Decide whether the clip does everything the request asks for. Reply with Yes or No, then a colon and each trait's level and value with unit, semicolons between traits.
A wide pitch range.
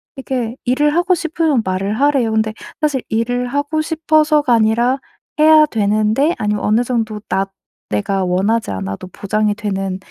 Yes: wide, 5.8 semitones